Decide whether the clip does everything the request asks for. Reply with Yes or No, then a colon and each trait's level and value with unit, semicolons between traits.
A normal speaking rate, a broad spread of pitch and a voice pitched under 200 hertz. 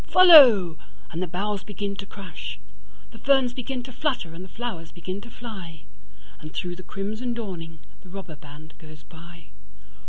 Yes: average, 155 wpm; wide, 5.7 semitones; medium, 185 Hz